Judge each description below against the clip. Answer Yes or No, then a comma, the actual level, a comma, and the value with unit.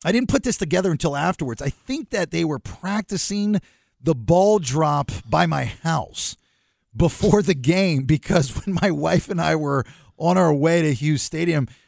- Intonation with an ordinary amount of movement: Yes, average, 4.6 semitones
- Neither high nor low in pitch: Yes, medium, 165 Hz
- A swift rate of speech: No, average, 175 wpm